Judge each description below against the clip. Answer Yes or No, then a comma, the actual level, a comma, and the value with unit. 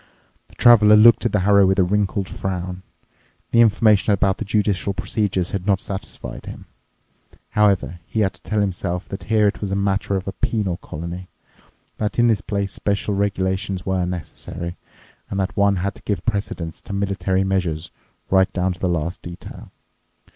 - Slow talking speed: No, average, 175 wpm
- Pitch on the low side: Yes, very low, 95 Hz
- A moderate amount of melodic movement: No, narrow, 1.9 semitones